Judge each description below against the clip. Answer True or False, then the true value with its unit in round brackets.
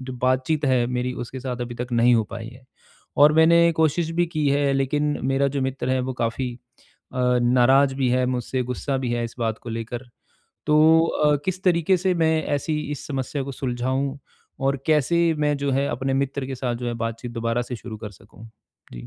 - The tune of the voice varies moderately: True (3.2 semitones)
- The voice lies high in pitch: False (130 Hz)